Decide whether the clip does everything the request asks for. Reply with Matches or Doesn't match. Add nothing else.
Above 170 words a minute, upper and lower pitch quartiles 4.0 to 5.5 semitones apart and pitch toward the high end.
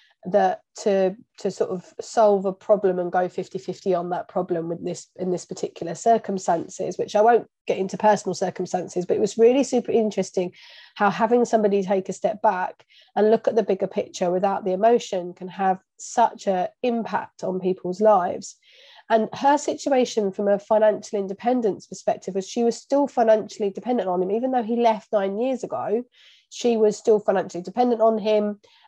Doesn't match